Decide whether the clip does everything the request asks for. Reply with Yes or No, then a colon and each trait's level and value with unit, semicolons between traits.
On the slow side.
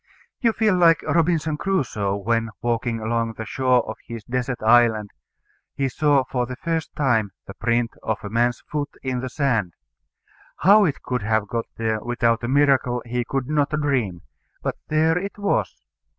No: average, 170 wpm